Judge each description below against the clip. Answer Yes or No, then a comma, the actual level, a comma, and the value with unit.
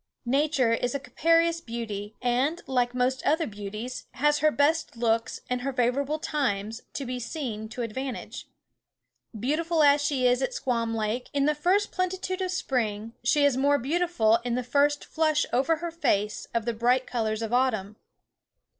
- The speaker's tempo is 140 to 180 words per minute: Yes, average, 170 wpm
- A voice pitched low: No, very high, 255 Hz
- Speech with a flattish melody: No, average, 4.3 semitones